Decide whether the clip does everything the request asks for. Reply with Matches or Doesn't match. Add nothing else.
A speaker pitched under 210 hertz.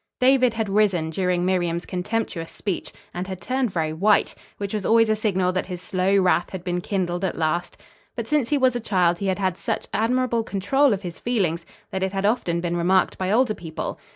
Matches